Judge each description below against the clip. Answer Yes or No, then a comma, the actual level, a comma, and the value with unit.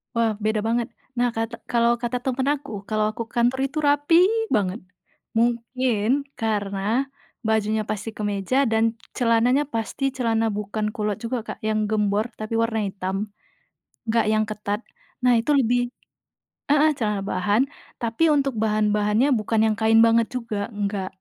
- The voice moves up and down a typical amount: No, narrow, 2.3 semitones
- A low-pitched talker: No, high, 225 Hz